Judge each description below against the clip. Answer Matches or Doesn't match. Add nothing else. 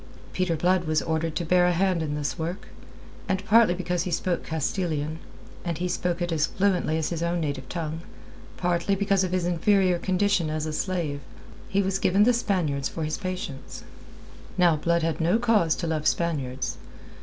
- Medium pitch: Matches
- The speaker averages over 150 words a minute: Matches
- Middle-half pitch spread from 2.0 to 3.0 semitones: Matches